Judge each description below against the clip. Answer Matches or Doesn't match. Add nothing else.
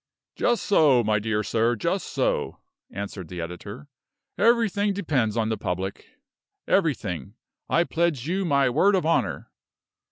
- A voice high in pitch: Doesn't match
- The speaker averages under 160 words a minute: Matches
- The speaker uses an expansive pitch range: Matches